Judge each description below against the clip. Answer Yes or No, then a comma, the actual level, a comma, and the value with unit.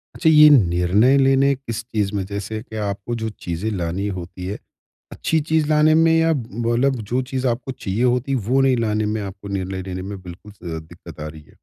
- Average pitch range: No, wide, 5.7 semitones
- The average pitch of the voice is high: No, low, 110 Hz